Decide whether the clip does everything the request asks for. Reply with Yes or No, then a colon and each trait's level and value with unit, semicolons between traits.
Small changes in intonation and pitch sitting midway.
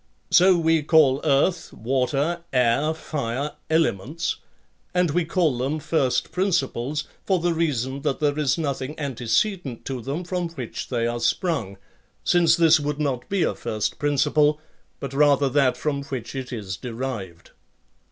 No: average, 4.2 semitones; medium, 145 Hz